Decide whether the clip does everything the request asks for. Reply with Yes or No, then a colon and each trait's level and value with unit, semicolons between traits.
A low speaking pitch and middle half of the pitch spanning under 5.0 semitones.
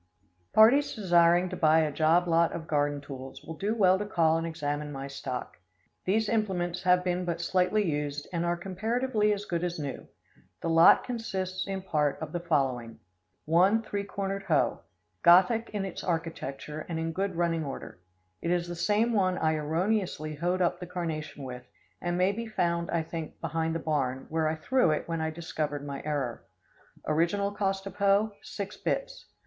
No: medium, 170 Hz; average, 3.8 semitones